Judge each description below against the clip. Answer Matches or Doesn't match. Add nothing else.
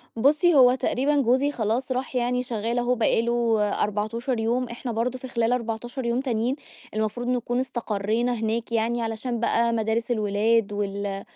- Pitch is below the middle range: Doesn't match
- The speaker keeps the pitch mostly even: Matches